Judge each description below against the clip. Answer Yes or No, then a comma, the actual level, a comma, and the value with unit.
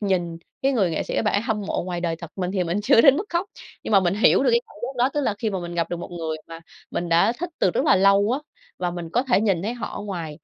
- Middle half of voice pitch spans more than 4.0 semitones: Yes, average, 5.0 semitones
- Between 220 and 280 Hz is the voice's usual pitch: No, high, 195 Hz